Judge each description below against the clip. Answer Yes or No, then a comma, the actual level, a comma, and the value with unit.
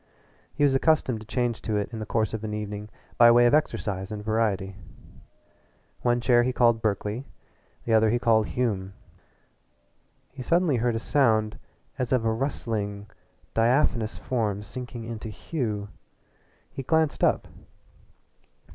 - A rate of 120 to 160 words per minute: Yes, average, 145 wpm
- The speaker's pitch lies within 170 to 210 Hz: No, low, 115 Hz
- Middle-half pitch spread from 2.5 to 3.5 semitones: Yes, average, 2.8 semitones